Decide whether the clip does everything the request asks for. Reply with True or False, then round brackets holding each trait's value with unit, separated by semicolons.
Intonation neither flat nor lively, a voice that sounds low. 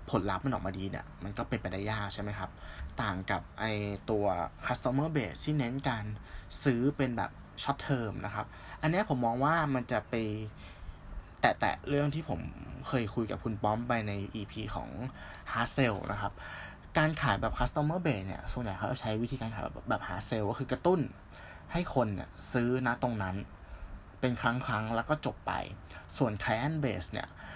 True (4.6 semitones; 110 Hz)